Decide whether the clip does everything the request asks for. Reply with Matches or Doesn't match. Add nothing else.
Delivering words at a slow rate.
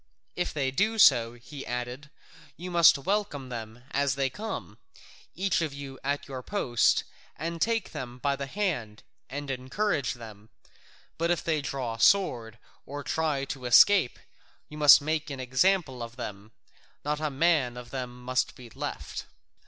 Doesn't match